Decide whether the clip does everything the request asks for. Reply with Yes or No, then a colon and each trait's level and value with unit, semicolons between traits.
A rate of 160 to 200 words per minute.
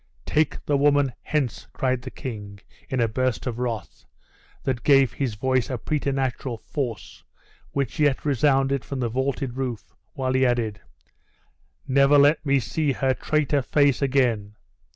No: average, 150 wpm